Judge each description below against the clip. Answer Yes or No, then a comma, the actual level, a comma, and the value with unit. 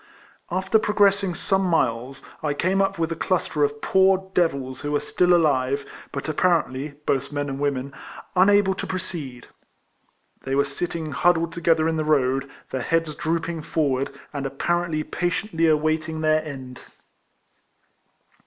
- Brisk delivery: No, average, 145 wpm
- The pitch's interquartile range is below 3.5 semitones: No, average, 4.0 semitones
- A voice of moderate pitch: Yes, medium, 155 Hz